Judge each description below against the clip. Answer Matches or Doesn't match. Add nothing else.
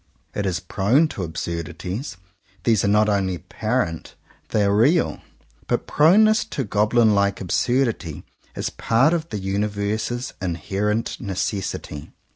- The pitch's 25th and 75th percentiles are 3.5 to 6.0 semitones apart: Matches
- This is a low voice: Matches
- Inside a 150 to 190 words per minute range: Doesn't match